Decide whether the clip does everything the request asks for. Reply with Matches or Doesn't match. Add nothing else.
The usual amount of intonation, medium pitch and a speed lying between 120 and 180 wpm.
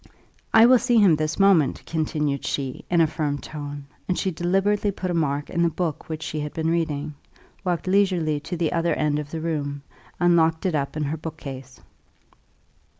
Doesn't match